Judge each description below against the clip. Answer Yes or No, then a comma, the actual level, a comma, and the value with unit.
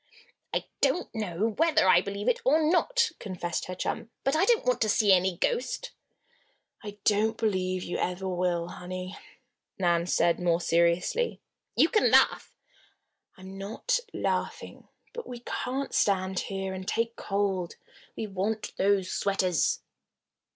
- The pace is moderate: Yes, average, 145 wpm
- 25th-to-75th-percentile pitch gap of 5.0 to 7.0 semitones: No, average, 4.5 semitones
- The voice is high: Yes, high, 195 Hz